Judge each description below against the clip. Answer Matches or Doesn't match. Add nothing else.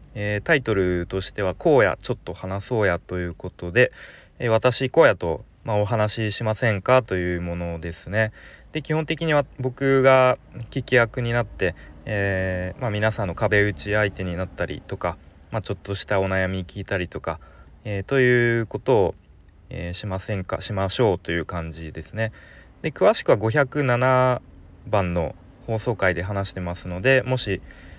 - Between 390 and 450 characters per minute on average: Doesn't match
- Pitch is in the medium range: Doesn't match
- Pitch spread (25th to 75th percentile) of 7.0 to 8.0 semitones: Doesn't match